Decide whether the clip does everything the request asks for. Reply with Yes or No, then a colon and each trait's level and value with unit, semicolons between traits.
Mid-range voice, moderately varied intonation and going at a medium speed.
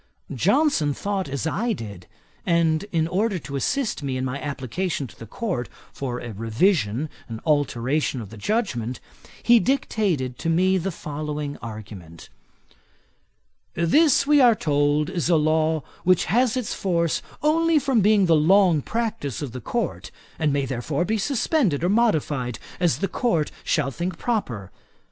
No: medium, 160 Hz; wide, 7.2 semitones; average, 155 wpm